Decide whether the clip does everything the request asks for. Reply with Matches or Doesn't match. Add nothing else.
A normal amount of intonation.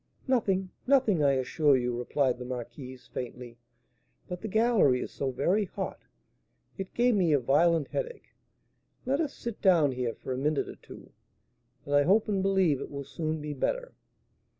Doesn't match